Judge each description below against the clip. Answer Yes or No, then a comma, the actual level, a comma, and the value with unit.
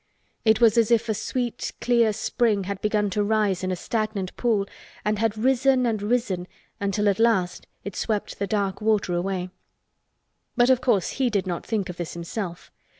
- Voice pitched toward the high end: Yes, high, 210 Hz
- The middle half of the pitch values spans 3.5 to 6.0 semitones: No, average, 3.1 semitones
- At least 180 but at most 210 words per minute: Yes, average, 185 wpm